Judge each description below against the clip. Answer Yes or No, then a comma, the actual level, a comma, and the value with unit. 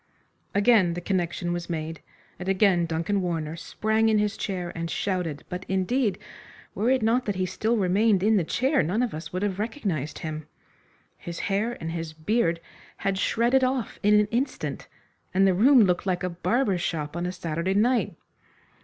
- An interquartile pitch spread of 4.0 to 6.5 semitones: Yes, average, 4.3 semitones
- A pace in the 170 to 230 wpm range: Yes, average, 180 wpm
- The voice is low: No, high, 190 Hz